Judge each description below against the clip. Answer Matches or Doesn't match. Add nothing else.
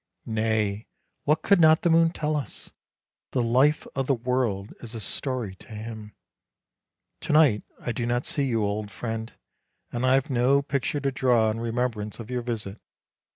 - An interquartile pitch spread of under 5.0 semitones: Matches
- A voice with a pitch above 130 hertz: Doesn't match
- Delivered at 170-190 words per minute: Matches